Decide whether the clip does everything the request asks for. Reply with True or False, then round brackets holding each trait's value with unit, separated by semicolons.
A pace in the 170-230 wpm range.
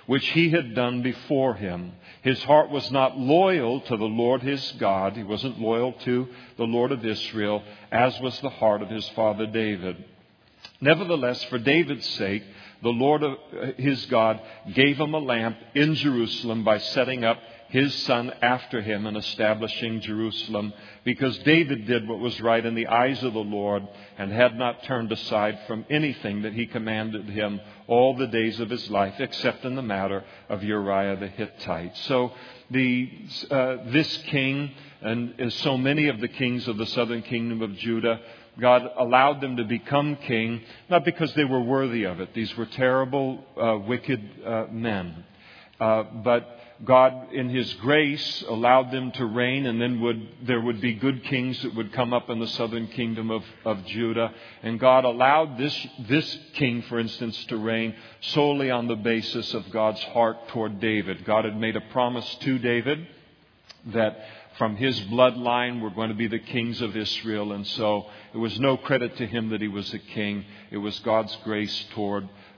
True (180 wpm)